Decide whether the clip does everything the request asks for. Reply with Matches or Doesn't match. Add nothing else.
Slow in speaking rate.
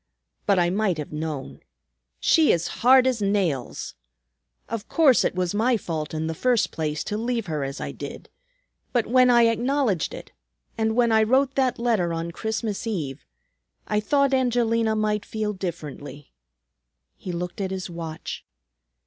Doesn't match